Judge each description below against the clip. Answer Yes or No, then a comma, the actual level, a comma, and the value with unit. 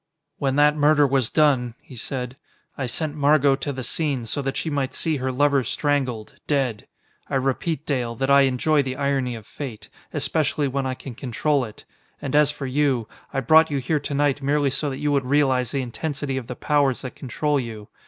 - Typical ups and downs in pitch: No, narrow, 2.3 semitones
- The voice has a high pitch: No, low, 135 Hz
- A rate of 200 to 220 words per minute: Yes, fast, 205 wpm